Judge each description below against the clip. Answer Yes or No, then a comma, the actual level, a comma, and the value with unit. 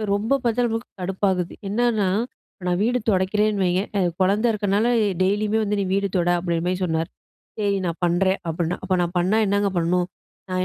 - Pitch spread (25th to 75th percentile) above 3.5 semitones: No, average, 2.8 semitones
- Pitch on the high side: Yes, high, 195 Hz